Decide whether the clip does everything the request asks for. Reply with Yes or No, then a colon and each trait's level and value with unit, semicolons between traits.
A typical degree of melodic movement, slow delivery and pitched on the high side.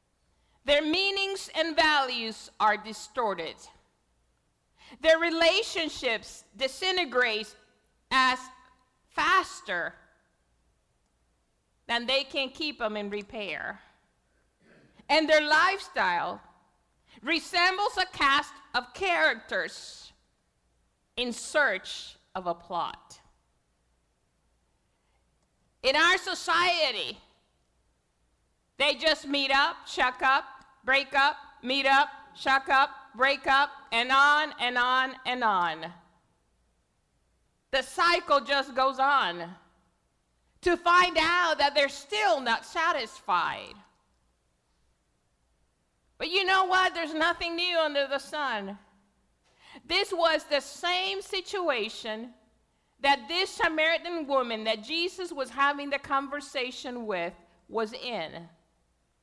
No: wide, 6.8 semitones; slow, 95 wpm; very high, 275 Hz